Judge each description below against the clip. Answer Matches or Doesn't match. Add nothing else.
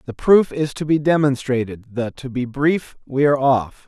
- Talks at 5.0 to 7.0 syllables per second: Doesn't match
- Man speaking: Matches